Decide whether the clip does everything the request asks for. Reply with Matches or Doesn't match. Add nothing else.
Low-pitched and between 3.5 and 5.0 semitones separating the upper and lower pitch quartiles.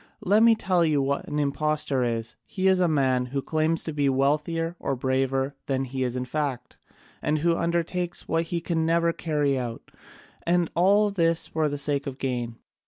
Doesn't match